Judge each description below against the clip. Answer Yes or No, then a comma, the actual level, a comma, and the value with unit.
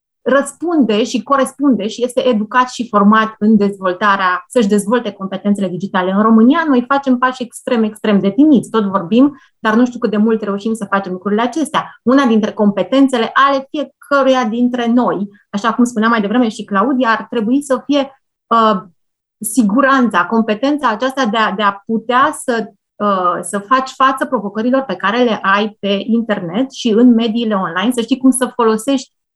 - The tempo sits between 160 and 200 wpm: Yes, fast, 170 wpm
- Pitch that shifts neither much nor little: Yes, average, 4.0 semitones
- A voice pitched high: Yes, high, 230 Hz